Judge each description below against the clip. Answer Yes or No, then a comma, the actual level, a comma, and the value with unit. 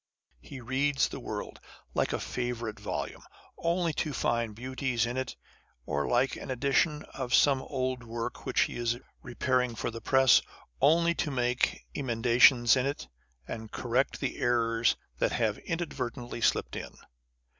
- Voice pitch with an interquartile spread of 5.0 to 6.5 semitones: No, narrow, 2.4 semitones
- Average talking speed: Yes, average, 150 wpm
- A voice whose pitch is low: Yes, low, 125 Hz